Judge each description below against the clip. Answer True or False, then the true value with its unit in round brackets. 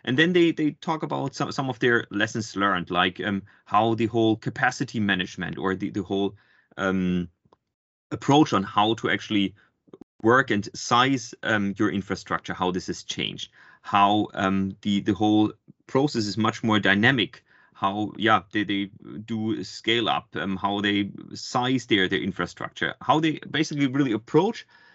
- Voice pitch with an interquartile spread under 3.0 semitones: False (4.2 semitones)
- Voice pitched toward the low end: True (105 Hz)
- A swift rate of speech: False (165 wpm)